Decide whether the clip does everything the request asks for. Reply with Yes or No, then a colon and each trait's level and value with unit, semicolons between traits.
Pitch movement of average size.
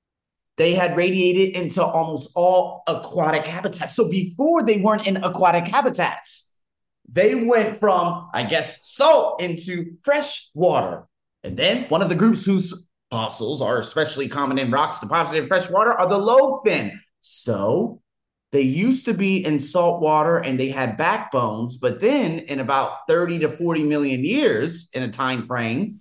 Yes: average, 4.4 semitones